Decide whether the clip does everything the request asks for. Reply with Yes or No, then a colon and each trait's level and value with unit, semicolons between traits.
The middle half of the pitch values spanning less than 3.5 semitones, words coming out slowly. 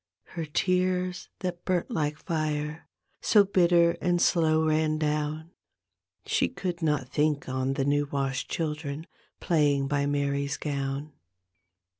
Yes: average, 3.1 semitones; slow, 125 wpm